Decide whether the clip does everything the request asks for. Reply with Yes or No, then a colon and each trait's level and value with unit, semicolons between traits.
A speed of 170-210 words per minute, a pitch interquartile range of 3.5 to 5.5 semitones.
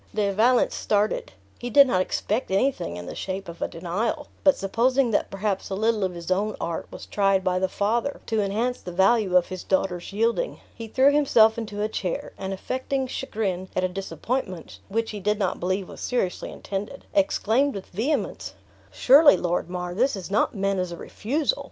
Yes: average, 195 wpm; average, 4.4 semitones